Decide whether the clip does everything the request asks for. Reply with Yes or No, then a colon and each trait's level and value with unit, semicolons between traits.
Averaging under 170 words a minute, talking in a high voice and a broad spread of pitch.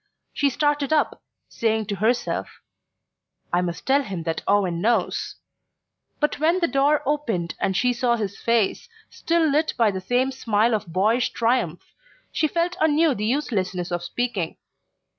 Yes: average, 155 wpm; high, 235 Hz; wide, 6.9 semitones